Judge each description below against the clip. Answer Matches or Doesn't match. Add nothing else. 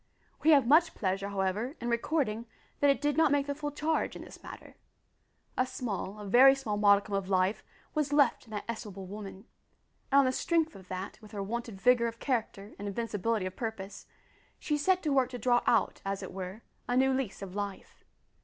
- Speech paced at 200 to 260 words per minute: Matches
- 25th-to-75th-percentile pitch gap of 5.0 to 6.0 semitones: Matches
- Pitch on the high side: Matches